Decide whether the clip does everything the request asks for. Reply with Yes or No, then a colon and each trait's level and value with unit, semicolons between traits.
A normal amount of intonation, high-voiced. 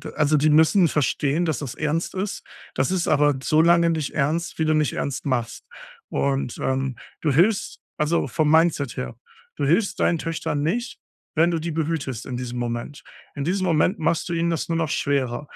No: average, 3.2 semitones; medium, 155 Hz